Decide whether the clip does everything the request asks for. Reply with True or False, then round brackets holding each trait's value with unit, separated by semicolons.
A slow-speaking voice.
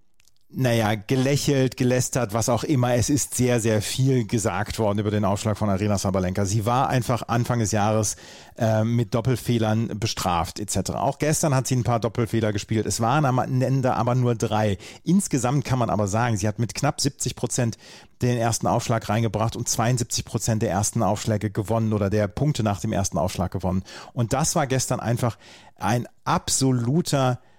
False (175 wpm)